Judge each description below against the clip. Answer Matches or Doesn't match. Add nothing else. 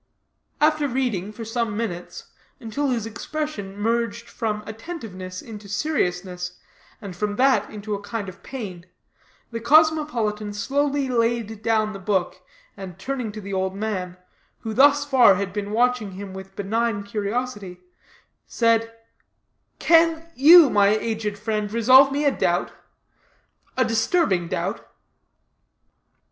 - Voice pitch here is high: Matches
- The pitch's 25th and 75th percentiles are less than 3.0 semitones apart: Doesn't match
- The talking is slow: Matches